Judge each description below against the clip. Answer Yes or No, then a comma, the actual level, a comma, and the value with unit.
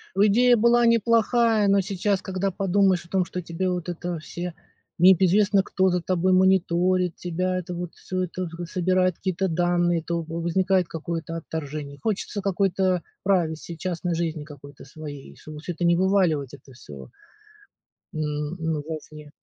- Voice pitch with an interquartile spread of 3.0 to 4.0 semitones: No, narrow, 2.6 semitones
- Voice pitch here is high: No, medium, 180 Hz